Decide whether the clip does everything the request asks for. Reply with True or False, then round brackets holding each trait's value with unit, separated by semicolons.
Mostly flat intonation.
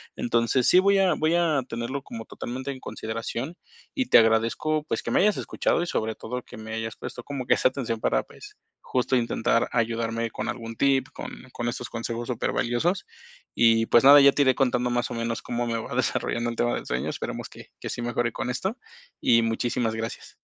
False (3.0 semitones)